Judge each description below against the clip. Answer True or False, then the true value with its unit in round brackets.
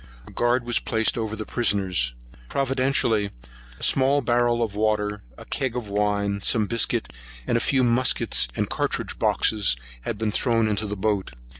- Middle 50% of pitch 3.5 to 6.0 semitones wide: False (2.7 semitones)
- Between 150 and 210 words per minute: True (165 wpm)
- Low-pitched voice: True (110 Hz)